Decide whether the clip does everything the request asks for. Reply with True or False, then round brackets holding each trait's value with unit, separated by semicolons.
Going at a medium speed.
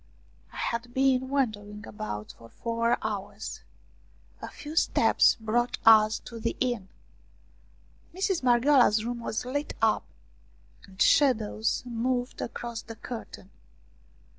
False (115 wpm)